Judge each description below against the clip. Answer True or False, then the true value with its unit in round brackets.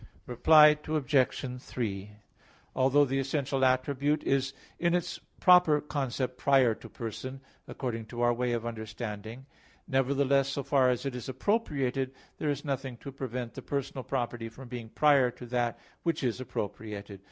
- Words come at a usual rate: True (150 wpm)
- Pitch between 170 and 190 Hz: False (130 Hz)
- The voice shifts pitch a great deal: False (2.7 semitones)